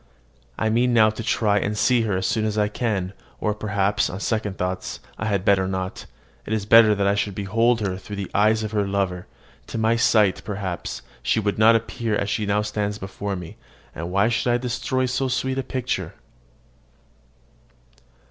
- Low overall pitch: Yes, low, 105 Hz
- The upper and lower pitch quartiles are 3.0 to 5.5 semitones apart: No, narrow, 2.4 semitones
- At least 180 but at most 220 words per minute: Yes, average, 190 wpm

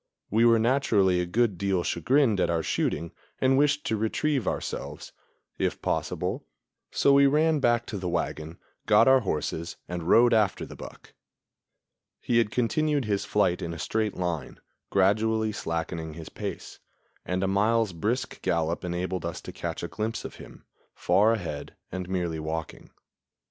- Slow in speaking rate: No, average, 160 wpm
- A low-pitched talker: Yes, low, 100 Hz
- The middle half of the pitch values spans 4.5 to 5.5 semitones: Yes, average, 5.2 semitones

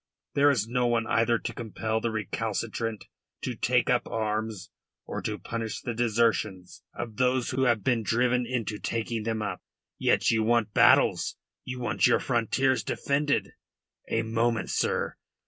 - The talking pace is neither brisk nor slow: Yes, average, 155 wpm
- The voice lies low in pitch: Yes, low, 115 Hz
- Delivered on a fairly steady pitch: Yes, narrow, 2.0 semitones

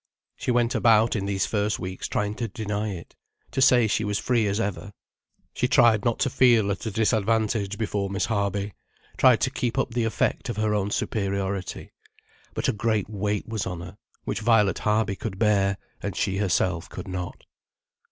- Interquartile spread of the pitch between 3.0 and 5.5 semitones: No, narrow, 2.4 semitones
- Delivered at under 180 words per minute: No, average, 185 wpm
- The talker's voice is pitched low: Yes, low, 105 Hz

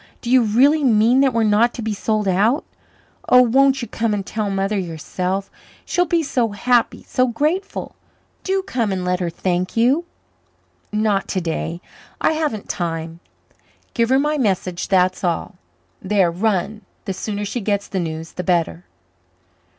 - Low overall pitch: No, high, 210 Hz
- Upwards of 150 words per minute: Yes, average, 160 wpm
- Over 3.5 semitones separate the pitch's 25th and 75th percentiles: Yes, average, 5.2 semitones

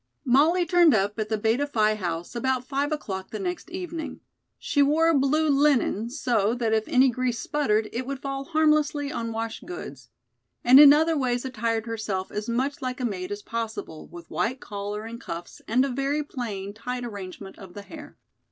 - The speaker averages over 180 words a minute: Yes, average, 190 wpm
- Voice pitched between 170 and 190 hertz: No, high, 245 Hz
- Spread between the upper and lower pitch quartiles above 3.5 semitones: Yes, average, 5.1 semitones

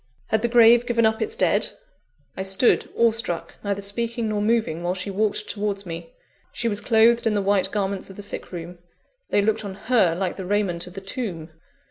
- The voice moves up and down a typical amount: Yes, average, 3.1 semitones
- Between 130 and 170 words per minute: No, fast, 205 wpm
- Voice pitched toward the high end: Yes, high, 205 Hz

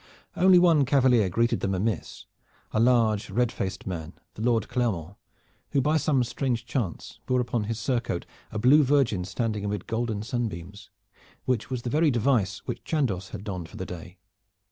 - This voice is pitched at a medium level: No, low, 115 Hz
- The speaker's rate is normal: Yes, average, 170 wpm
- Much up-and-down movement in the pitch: No, average, 4.4 semitones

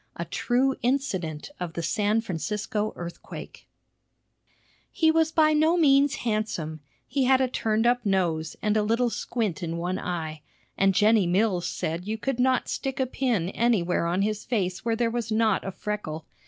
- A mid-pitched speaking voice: No, high, 215 Hz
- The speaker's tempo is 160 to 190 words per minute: Yes, average, 170 wpm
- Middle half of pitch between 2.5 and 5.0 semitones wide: No, wide, 5.6 semitones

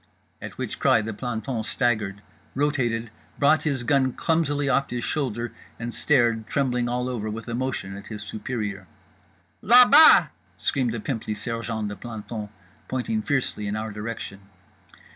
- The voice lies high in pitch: No, low, 120 Hz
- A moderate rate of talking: Yes, average, 150 wpm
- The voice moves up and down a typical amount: Yes, average, 3.8 semitones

